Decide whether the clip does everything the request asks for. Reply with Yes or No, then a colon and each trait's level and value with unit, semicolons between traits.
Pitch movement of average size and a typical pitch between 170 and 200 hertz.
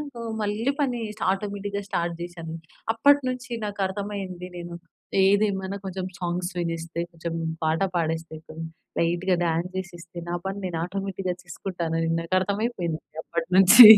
Yes: average, 3.0 semitones; medium, 185 Hz